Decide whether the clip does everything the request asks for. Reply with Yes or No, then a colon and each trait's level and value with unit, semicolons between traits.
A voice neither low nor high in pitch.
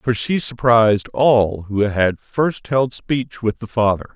No: low, 115 Hz